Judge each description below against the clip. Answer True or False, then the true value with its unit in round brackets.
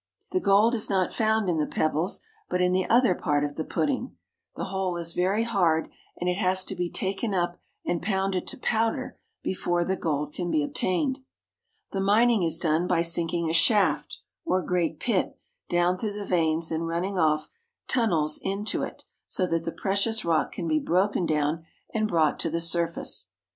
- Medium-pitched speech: True (180 Hz)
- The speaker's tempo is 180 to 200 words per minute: True (185 wpm)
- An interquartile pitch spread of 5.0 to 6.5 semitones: False (3.2 semitones)